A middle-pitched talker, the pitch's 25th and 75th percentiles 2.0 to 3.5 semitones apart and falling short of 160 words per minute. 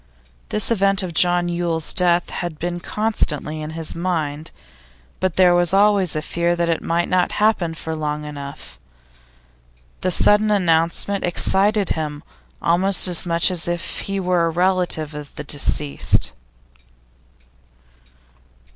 Yes: medium, 175 Hz; narrow, 2.6 semitones; average, 140 wpm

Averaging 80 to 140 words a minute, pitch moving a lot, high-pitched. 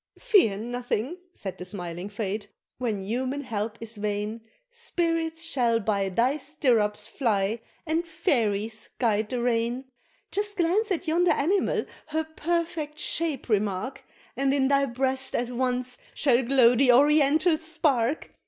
Yes: slow, 135 wpm; wide, 6.1 semitones; very high, 255 Hz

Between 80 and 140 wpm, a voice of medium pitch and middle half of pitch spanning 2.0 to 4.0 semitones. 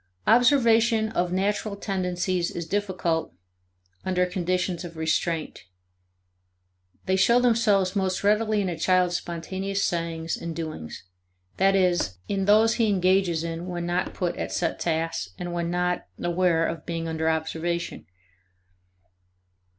Yes: slow, 135 wpm; medium, 180 Hz; average, 2.8 semitones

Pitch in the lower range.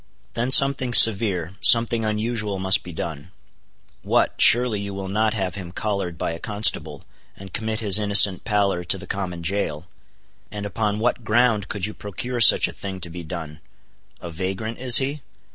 Yes: low, 100 Hz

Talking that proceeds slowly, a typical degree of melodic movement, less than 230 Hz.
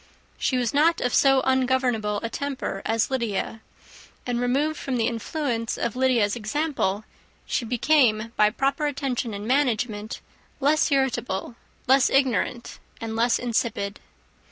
No: slow, 130 wpm; average, 3.4 semitones; high, 245 Hz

